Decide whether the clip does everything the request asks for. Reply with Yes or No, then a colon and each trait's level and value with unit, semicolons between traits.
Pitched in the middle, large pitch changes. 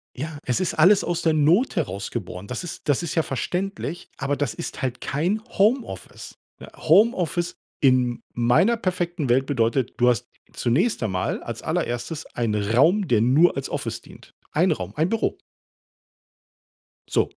Yes: medium, 145 Hz; wide, 6.5 semitones